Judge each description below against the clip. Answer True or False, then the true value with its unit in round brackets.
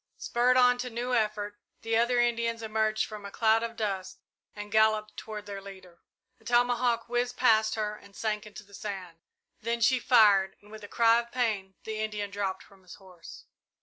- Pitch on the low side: False (215 Hz)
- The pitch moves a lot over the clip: False (2.5 semitones)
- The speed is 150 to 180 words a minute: False (190 wpm)